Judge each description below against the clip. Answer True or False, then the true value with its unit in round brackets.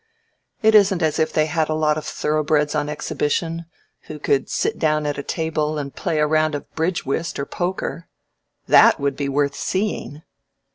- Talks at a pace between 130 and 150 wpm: False (185 wpm)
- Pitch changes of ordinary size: False (1.8 semitones)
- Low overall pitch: False (155 Hz)